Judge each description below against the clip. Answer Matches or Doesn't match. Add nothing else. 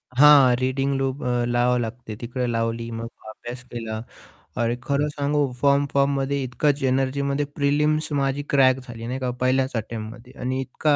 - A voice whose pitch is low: Matches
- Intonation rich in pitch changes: Doesn't match